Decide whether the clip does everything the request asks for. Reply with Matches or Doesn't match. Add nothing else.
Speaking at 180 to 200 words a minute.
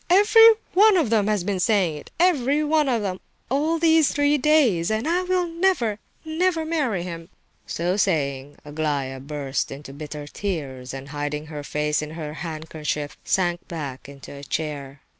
Doesn't match